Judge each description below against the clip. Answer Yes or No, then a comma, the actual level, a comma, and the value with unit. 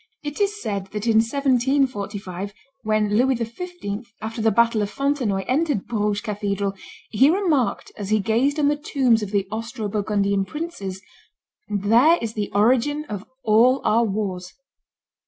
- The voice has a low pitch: No, high, 220 Hz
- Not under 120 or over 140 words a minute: No, average, 150 wpm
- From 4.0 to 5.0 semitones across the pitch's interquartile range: Yes, average, 4.5 semitones